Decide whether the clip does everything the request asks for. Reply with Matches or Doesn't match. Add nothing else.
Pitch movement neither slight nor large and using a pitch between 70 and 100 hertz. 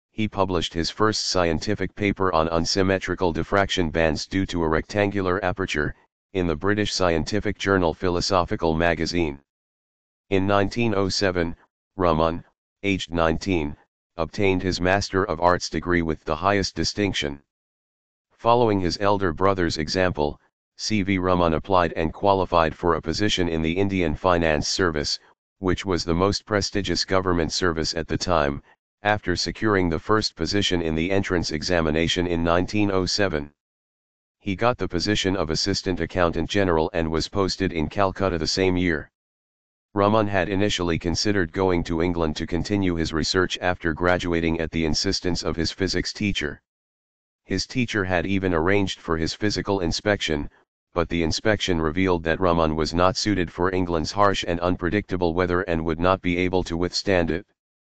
Matches